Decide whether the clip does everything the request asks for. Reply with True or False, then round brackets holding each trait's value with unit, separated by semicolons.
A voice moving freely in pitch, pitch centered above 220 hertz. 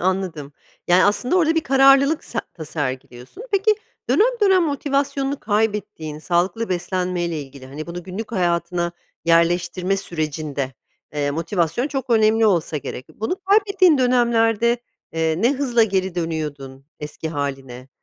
False (7.7 semitones; 185 Hz)